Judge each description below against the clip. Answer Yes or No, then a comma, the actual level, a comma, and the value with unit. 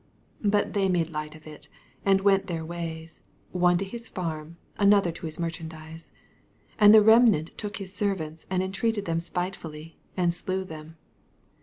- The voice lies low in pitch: No, medium, 175 Hz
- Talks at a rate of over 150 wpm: Yes, average, 180 wpm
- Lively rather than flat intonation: No, average, 3.5 semitones